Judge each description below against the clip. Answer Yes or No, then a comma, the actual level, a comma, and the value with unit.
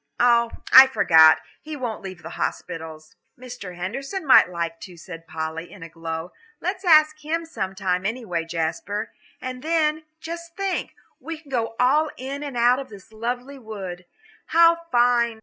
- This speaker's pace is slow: No, average, 155 wpm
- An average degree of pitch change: No, wide, 8.1 semitones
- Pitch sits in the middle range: No, high, 235 Hz